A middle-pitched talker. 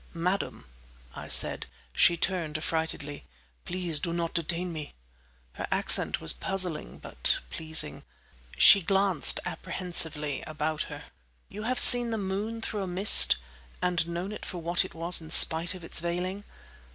Yes: medium, 170 Hz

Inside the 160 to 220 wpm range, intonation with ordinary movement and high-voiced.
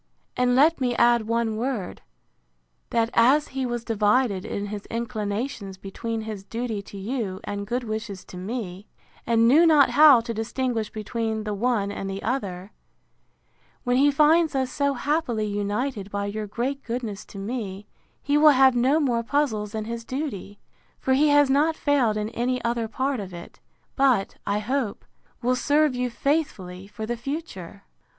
Yes: average, 170 wpm; average, 4.4 semitones; high, 235 Hz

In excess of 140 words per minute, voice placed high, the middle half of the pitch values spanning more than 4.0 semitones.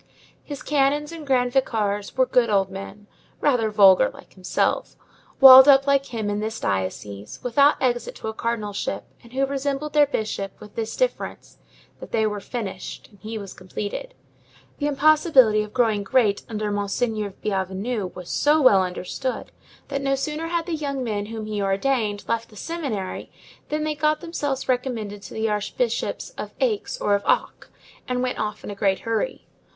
Yes: average, 175 wpm; high, 230 Hz; average, 5.2 semitones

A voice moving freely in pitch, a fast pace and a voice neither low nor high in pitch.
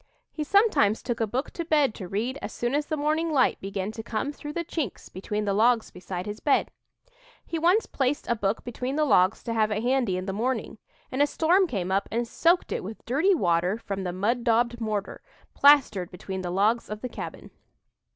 No: wide, 6.3 semitones; fast, 215 wpm; high, 235 Hz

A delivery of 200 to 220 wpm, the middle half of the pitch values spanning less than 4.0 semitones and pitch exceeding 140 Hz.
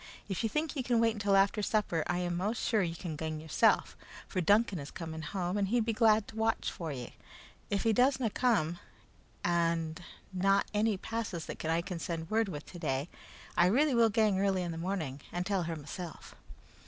No: fast, 205 wpm; average, 4.8 semitones; high, 190 Hz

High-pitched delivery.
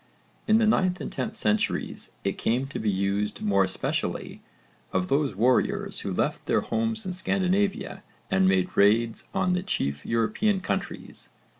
No: low, 125 Hz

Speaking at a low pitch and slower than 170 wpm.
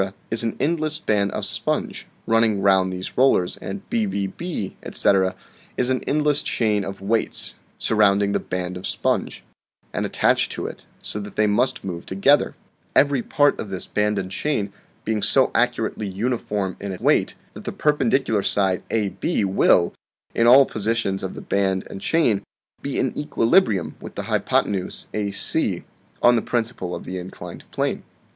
Yes: low, 105 Hz; average, 160 wpm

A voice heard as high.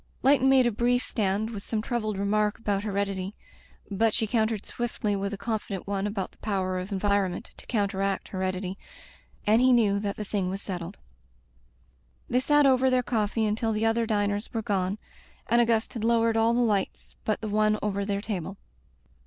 Yes: high, 210 Hz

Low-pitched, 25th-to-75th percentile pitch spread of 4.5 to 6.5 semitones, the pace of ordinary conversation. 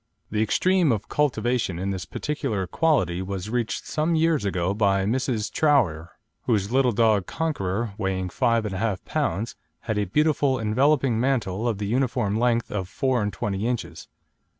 Yes: low, 110 Hz; average, 5.1 semitones; average, 155 wpm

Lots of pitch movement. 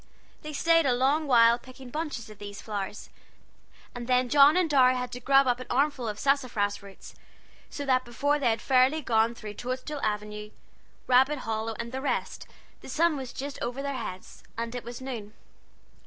No: average, 3.4 semitones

